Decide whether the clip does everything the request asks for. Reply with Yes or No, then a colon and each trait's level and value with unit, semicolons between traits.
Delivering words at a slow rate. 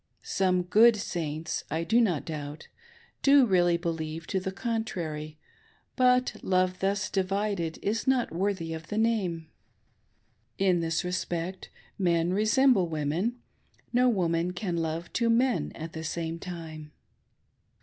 Yes: slow, 130 wpm